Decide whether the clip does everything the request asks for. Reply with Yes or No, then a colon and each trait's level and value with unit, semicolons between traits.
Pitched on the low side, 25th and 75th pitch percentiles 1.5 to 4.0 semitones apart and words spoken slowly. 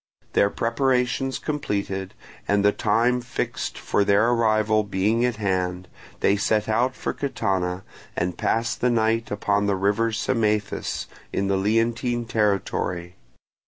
Yes: low, 110 Hz; average, 2.9 semitones; slow, 130 wpm